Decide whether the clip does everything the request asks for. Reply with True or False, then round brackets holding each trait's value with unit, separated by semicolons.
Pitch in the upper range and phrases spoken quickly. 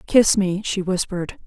False (195 Hz; 165 wpm)